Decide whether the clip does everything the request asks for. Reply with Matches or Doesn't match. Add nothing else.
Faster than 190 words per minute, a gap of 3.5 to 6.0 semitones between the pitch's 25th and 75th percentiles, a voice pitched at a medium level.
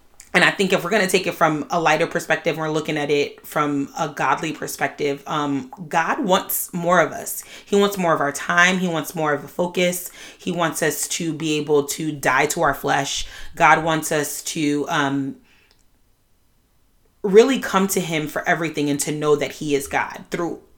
Doesn't match